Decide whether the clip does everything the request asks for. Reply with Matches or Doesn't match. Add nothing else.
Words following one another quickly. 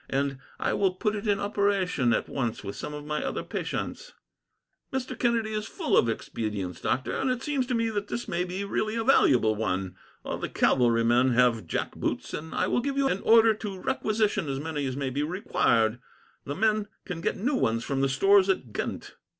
Matches